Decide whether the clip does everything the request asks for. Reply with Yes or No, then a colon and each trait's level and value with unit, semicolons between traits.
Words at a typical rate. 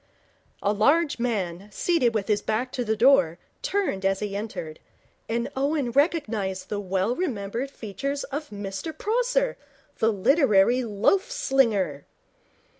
No: slow, 130 wpm